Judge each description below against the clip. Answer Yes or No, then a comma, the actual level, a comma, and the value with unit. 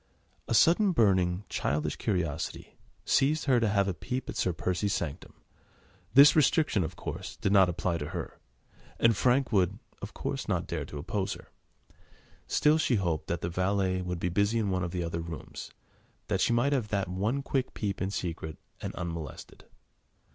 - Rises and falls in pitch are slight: No, average, 5.2 semitones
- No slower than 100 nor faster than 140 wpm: No, average, 180 wpm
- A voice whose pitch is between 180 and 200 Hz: No, very low, 95 Hz